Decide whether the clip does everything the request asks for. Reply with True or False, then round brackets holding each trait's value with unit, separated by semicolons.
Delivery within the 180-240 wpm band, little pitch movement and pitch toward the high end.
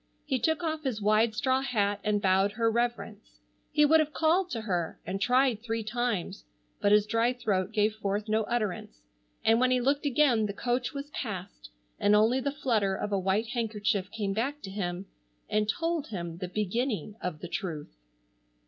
False (185 wpm; 4.1 semitones; 220 Hz)